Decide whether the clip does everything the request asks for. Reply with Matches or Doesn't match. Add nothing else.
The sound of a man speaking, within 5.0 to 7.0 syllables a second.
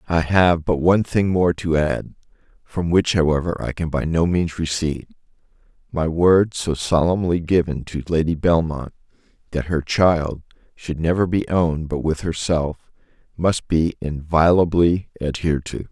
Doesn't match